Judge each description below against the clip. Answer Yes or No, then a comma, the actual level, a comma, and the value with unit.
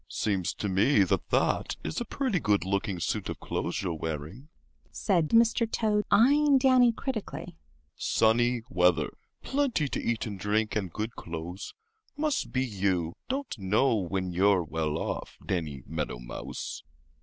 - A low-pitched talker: Yes, low, 105 Hz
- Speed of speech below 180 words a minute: Yes, average, 145 wpm